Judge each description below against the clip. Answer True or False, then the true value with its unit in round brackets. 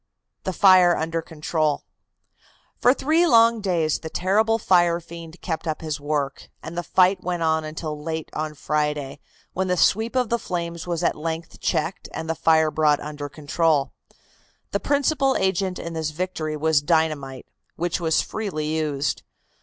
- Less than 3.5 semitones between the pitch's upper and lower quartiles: True (3.1 semitones)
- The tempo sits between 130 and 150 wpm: False (160 wpm)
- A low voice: False (165 Hz)